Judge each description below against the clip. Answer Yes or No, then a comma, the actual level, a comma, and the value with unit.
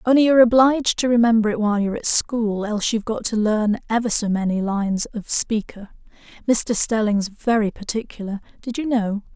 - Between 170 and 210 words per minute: Yes, average, 175 wpm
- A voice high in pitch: Yes, high, 220 Hz